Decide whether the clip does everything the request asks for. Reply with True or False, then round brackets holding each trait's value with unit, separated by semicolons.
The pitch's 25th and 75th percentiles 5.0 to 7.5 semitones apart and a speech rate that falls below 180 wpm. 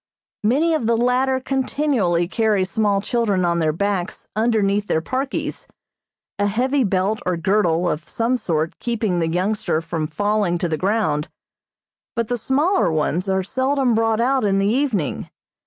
True (5.4 semitones; 155 wpm)